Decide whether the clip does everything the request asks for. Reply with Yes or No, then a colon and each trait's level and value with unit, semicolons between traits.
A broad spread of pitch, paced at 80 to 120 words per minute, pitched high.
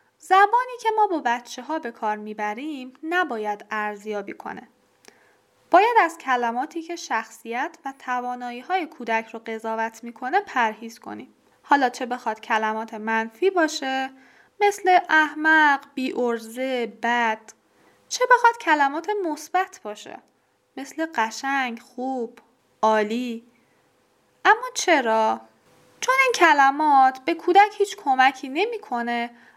Yes: wide, 6.7 semitones; average, 115 wpm; very high, 260 Hz